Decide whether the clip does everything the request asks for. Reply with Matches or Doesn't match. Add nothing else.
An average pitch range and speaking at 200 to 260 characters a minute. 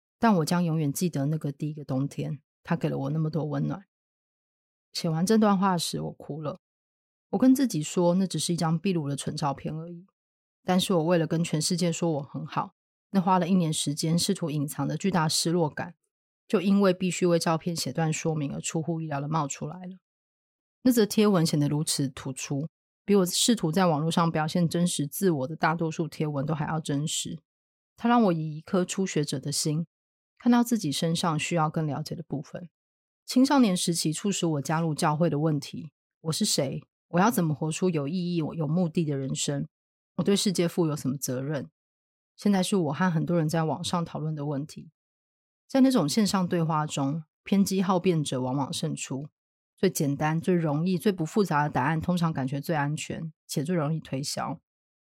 Doesn't match